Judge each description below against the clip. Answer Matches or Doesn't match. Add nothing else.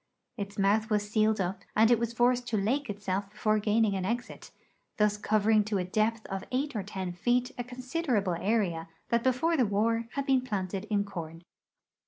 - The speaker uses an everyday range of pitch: Matches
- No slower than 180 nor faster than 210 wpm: Matches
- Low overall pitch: Doesn't match